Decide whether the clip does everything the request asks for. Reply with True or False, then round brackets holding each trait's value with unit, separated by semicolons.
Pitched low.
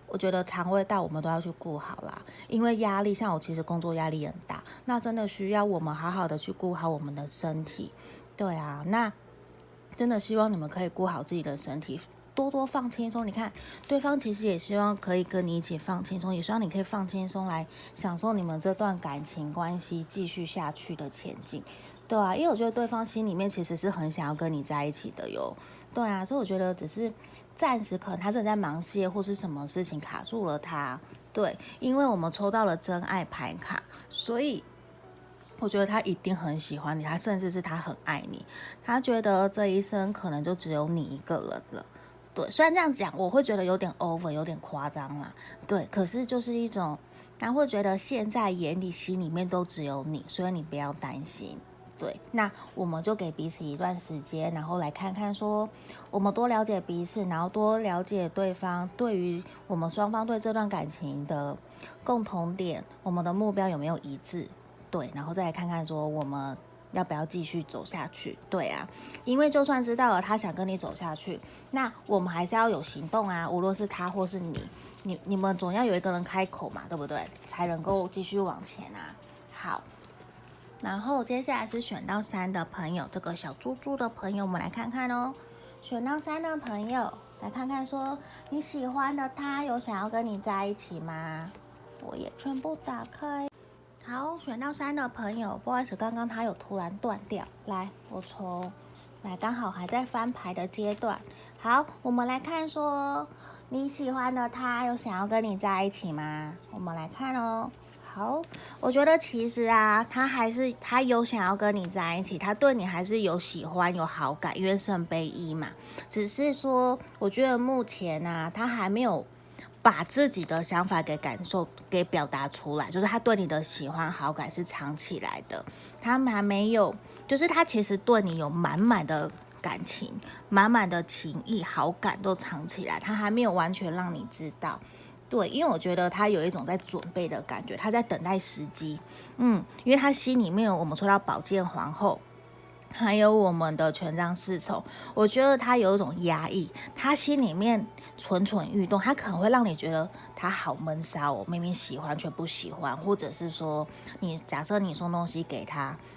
False (190 Hz)